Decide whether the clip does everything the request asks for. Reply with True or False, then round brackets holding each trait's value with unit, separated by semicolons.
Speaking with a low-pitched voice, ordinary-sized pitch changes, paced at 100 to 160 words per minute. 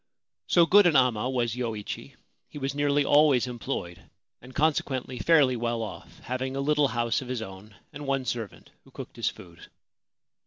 False (130 Hz; 3.4 semitones; 170 wpm)